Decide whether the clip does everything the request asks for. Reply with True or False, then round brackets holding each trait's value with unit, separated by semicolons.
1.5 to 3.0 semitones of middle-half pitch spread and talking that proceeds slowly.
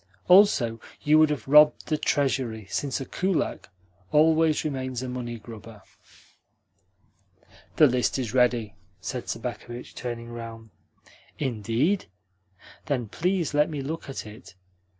False (4.5 semitones; 125 wpm)